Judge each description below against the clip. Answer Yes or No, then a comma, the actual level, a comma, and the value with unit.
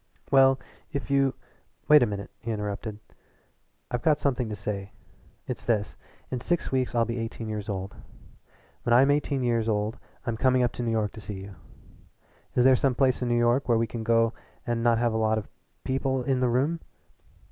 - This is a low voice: Yes, low, 120 Hz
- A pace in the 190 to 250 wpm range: Yes, average, 200 wpm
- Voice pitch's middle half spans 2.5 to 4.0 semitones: Yes, average, 3.0 semitones